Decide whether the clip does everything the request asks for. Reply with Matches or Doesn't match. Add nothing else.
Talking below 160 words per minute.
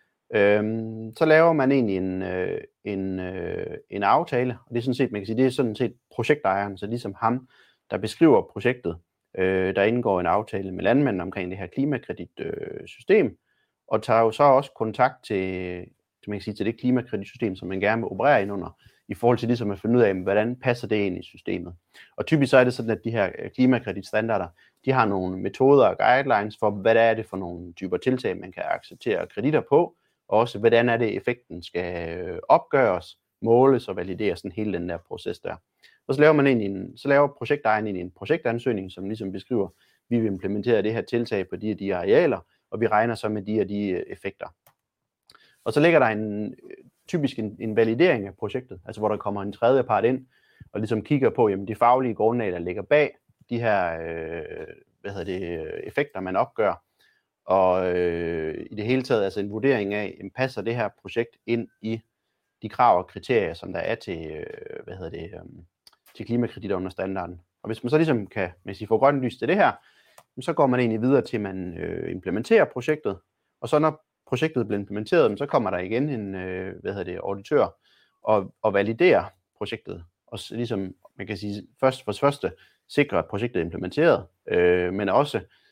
Doesn't match